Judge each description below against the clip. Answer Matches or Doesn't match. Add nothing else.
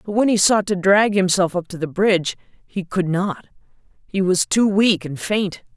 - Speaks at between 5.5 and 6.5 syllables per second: Doesn't match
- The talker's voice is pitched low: Doesn't match